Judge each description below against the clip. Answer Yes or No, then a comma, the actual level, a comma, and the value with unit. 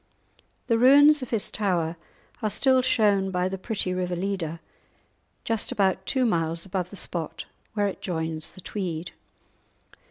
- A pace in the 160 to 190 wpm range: No, average, 150 wpm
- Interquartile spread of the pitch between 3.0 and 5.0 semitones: Yes, average, 4.1 semitones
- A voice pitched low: No, high, 190 Hz